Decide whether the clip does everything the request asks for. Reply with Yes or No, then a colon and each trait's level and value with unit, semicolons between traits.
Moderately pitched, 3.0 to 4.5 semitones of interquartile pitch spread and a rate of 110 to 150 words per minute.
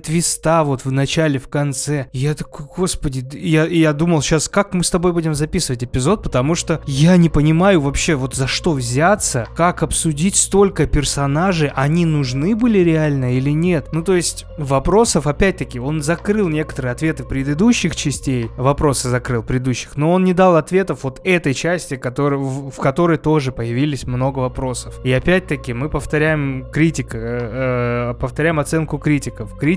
No: medium, 150 Hz; average, 4.0 semitones; fast, 160 wpm